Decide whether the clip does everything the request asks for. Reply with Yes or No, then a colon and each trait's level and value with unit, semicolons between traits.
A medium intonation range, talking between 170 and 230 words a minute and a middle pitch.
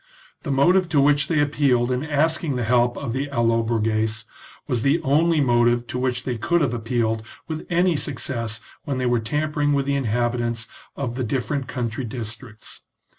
No: average, 3.6 semitones; average, 175 wpm; low, 125 Hz